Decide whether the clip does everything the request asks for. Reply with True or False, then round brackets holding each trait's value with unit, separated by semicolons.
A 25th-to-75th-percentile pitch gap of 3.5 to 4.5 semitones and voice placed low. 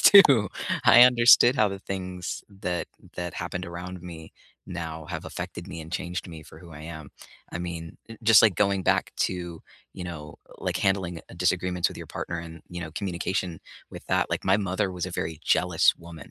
False (2.4 semitones; 90 Hz)